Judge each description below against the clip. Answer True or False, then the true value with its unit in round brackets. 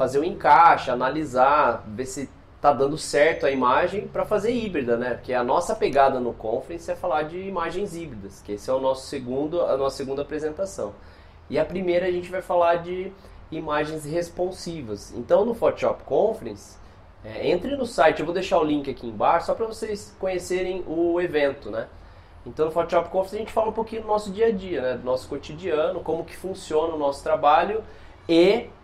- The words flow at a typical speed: False (195 wpm)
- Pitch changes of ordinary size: False (6.0 semitones)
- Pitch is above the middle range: False (155 Hz)